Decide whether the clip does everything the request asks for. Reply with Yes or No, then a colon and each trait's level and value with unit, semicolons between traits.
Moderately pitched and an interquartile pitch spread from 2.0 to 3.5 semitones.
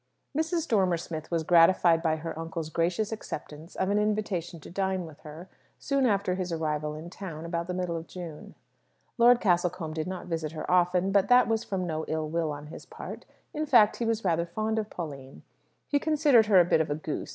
No: medium, 175 Hz; average, 4.3 semitones